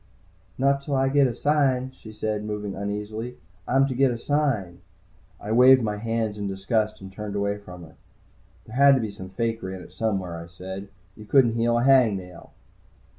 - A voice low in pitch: Yes, low, 110 Hz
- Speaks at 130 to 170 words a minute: No, average, 195 wpm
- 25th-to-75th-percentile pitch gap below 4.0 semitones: No, average, 4.3 semitones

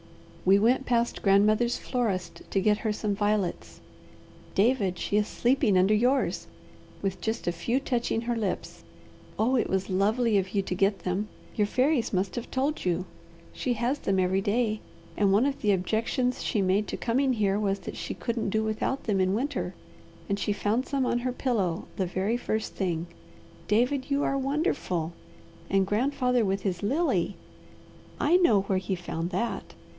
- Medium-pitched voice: No, high, 215 Hz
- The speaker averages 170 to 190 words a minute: Yes, average, 175 wpm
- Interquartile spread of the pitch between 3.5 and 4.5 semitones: Yes, average, 4.2 semitones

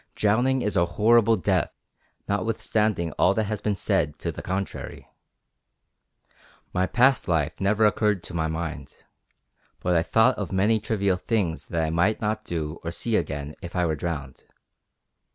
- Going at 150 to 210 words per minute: Yes, average, 160 wpm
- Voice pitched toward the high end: No, very low, 95 Hz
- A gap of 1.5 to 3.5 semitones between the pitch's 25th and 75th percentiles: No, average, 4.5 semitones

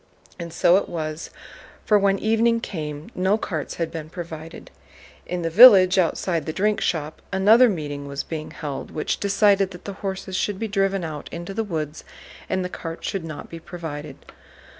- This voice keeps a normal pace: Yes, average, 180 wpm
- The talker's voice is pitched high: No, medium, 175 Hz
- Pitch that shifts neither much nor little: Yes, average, 3.9 semitones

